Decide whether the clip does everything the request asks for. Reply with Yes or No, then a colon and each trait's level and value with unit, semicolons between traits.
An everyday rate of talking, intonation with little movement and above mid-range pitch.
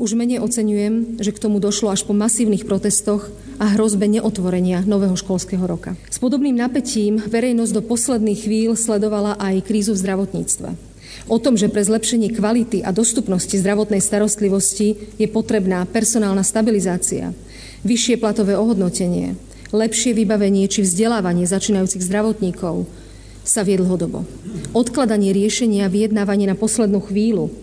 Yes: average, 130 wpm; narrow, 2.2 semitones; high, 210 Hz